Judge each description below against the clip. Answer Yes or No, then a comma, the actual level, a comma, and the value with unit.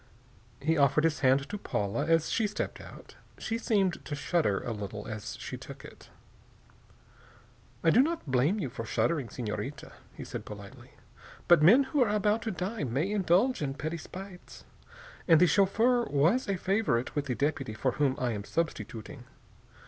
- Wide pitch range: Yes, wide, 7.3 semitones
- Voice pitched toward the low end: No, medium, 160 Hz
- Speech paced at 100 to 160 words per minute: No, average, 170 wpm